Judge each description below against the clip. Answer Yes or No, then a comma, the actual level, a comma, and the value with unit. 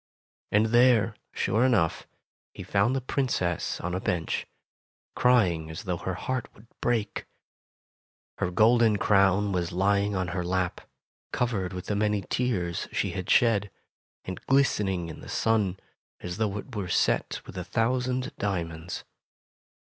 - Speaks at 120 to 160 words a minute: Yes, average, 145 wpm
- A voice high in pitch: No, low, 100 Hz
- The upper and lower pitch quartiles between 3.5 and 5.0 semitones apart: Yes, average, 4.3 semitones